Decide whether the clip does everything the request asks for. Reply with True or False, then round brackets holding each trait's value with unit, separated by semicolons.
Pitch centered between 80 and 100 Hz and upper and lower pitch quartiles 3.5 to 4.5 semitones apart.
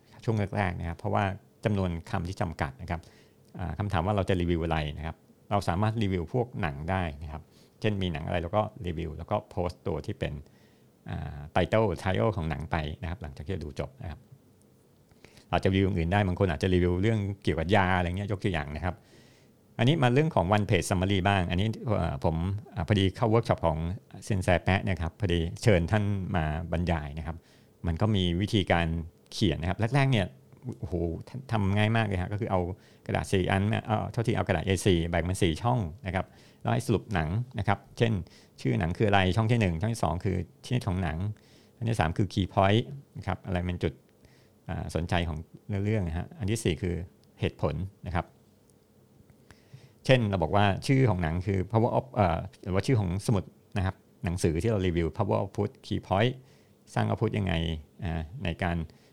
True (95 Hz; 4.1 semitones)